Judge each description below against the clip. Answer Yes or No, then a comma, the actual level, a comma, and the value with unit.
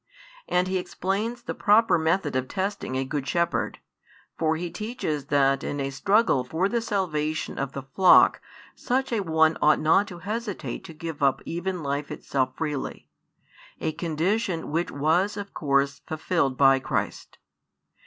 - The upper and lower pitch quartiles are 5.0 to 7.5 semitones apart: Yes, wide, 5.4 semitones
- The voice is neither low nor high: Yes, medium, 160 Hz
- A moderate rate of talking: Yes, average, 155 wpm